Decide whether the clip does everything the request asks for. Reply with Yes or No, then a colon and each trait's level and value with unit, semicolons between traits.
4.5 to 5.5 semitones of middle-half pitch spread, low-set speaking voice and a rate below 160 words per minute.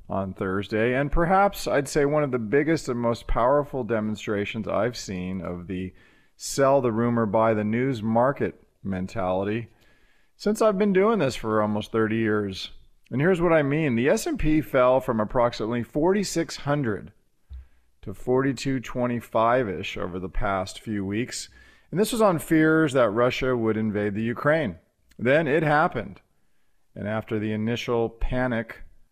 Yes: average, 4.9 semitones; low, 115 Hz; average, 150 wpm